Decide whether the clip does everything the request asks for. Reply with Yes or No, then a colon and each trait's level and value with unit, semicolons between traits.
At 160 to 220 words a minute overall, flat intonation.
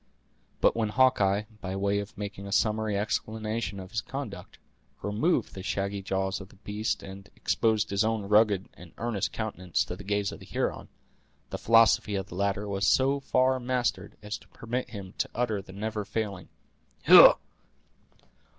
Yes: average, 170 wpm; narrow, 2.2 semitones